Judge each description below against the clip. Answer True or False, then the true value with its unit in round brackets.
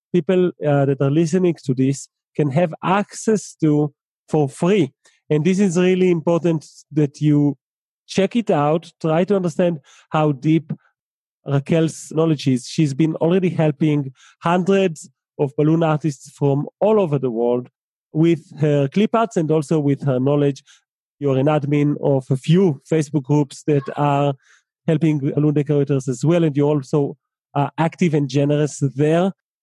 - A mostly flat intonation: False (3.0 semitones)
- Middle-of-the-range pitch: True (155 Hz)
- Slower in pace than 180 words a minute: True (160 wpm)